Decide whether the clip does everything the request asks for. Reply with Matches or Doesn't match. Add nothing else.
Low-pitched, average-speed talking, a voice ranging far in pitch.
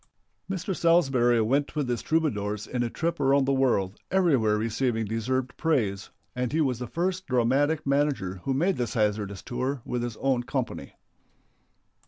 Doesn't match